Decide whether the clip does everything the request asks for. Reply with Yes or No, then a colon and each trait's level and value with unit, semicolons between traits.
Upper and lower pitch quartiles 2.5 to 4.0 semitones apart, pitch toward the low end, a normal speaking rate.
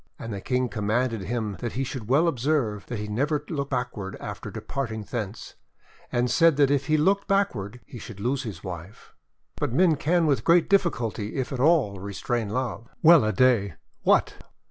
No: average, 5.2 semitones; low, 125 Hz; average, 185 wpm